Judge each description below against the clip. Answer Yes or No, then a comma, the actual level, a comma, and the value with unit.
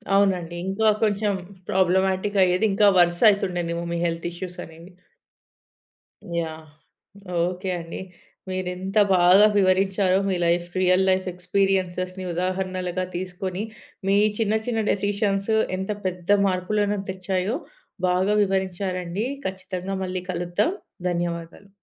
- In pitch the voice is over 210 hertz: No, medium, 185 Hz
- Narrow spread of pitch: Yes, narrow, 1.7 semitones